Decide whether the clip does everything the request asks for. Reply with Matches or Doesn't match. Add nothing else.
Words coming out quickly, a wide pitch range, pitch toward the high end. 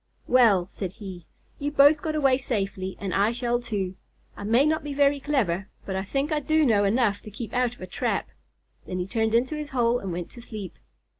Matches